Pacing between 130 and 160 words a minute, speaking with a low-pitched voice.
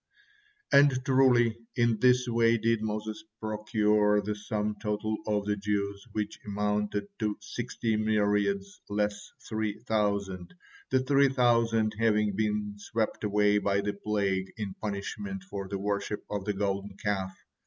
Yes: average, 140 wpm; low, 105 Hz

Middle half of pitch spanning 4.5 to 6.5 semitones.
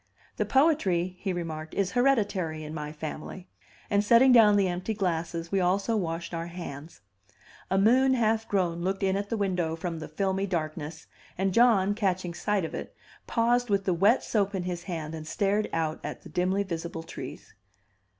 No: average, 3.6 semitones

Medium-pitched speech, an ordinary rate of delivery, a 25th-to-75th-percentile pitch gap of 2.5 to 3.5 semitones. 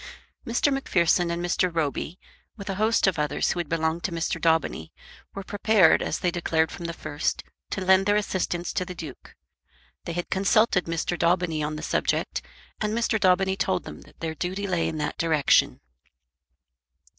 Yes: medium, 175 Hz; average, 180 wpm; average, 2.9 semitones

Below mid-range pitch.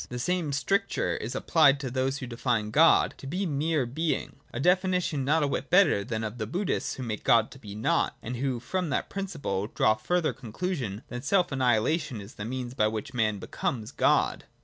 Yes: low, 130 Hz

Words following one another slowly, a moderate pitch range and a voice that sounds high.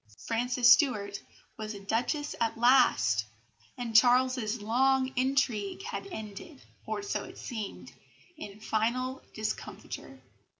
Yes: slow, 115 wpm; average, 3.4 semitones; high, 240 Hz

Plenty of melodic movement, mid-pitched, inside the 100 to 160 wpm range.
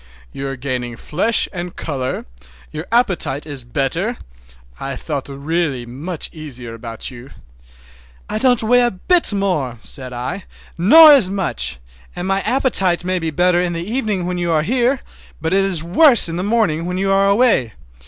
No: wide, 6.4 semitones; medium, 175 Hz; average, 175 wpm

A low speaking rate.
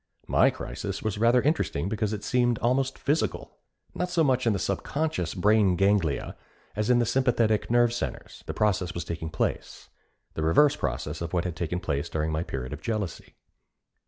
No: average, 180 wpm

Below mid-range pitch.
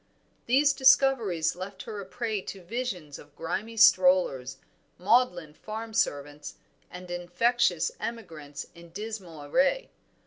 No: high, 190 Hz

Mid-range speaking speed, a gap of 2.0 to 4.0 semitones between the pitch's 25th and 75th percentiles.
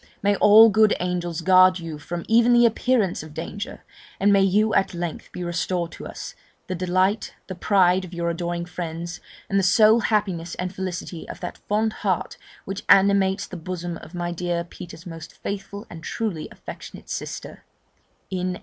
Yes: average, 175 wpm; average, 2.7 semitones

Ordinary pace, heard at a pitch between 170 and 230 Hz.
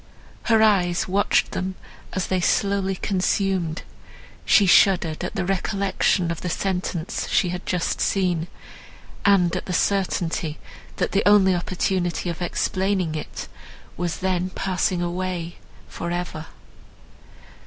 No: slow, 125 wpm; medium, 185 Hz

